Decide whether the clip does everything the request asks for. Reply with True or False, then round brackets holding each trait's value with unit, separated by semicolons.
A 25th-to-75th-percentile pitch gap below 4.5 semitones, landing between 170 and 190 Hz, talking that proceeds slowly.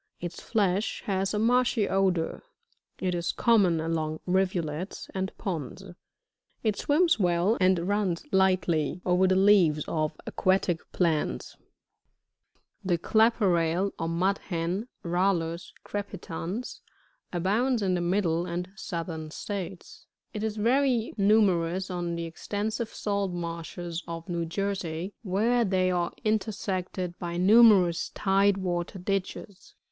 True (3.0 semitones; 185 Hz; 125 wpm)